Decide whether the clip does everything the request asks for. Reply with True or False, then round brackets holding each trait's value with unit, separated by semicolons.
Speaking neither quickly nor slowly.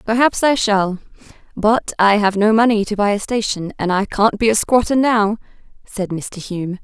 True (195 wpm)